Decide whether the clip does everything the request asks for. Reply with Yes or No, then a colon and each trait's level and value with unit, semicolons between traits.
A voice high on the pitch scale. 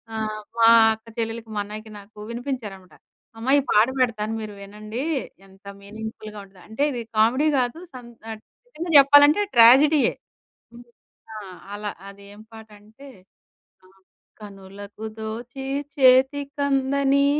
Yes: high, 225 Hz